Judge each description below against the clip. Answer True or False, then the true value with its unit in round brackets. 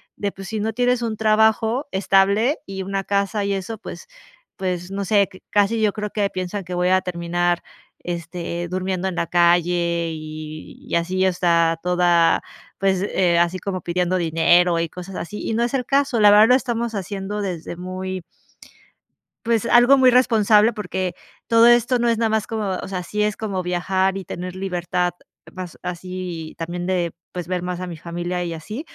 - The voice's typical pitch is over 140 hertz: True (185 Hz)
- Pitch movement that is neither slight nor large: True (3.1 semitones)